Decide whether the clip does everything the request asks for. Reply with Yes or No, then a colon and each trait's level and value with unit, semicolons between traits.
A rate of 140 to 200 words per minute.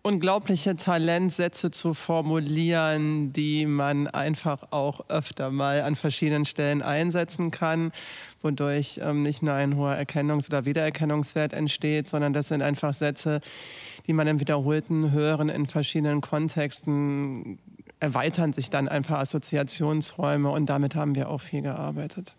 No: average, 130 wpm